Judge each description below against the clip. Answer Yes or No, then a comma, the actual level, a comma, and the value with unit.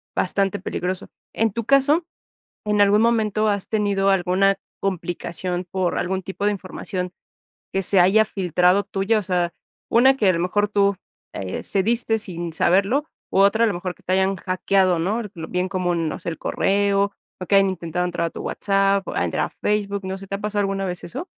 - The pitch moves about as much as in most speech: No, narrow, 2.3 semitones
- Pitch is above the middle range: Yes, high, 195 Hz